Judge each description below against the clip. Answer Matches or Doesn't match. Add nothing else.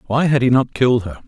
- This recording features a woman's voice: Doesn't match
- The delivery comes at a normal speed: Doesn't match